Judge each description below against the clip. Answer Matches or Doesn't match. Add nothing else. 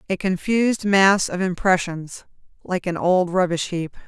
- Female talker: Matches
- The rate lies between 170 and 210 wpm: Doesn't match